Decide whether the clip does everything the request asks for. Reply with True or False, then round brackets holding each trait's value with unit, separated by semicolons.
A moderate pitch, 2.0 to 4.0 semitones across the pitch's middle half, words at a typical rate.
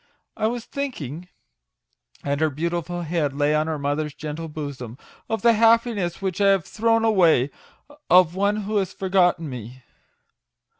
False (175 Hz; 5.4 semitones; 155 wpm)